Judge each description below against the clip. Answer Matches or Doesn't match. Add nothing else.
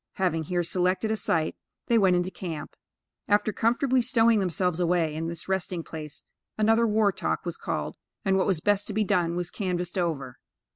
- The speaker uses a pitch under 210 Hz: Matches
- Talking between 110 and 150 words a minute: Doesn't match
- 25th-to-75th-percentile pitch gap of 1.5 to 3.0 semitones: Doesn't match